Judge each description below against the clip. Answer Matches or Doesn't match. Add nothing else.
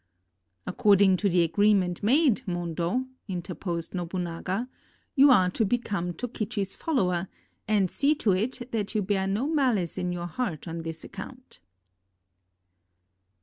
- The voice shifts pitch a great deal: Doesn't match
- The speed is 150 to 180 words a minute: Doesn't match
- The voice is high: Matches